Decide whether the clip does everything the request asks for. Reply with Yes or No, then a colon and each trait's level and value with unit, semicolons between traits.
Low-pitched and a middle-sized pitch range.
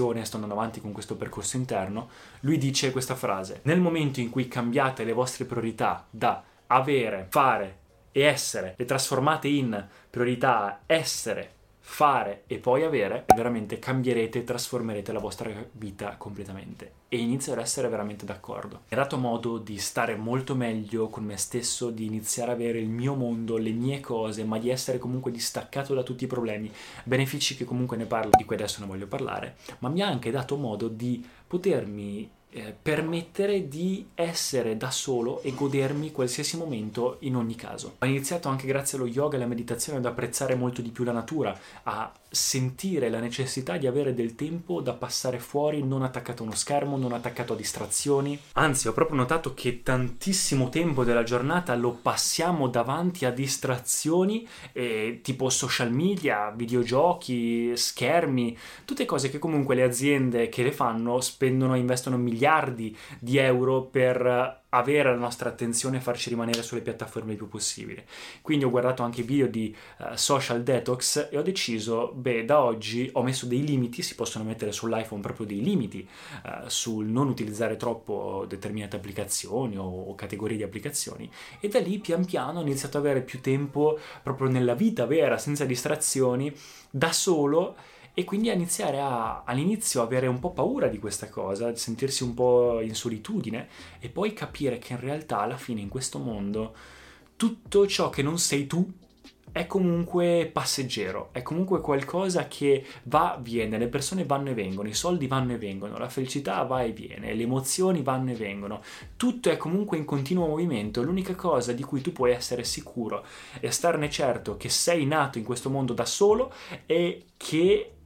Yes: low, 125 Hz; average, 3.6 semitones